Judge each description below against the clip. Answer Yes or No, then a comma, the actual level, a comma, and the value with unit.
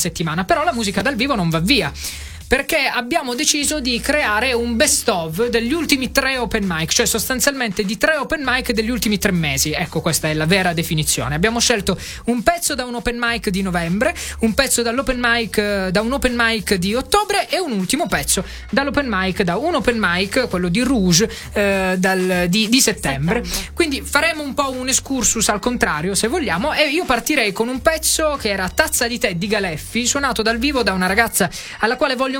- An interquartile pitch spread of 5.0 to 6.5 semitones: Yes, wide, 5.5 semitones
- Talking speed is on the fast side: Yes, fast, 200 wpm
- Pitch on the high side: Yes, high, 230 Hz